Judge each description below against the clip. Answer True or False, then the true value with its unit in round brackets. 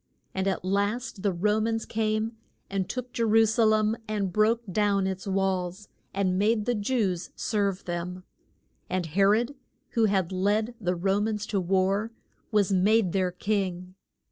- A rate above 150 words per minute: True (165 wpm)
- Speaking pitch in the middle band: False (200 Hz)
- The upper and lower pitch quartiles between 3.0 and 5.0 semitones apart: False (2.5 semitones)